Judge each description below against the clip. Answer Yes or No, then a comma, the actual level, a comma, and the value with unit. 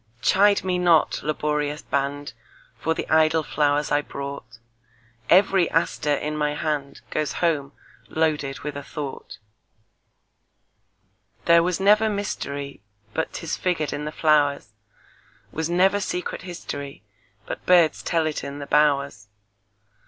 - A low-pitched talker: No, medium, 150 Hz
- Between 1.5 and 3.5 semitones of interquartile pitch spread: Yes, average, 3.2 semitones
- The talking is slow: Yes, slow, 110 wpm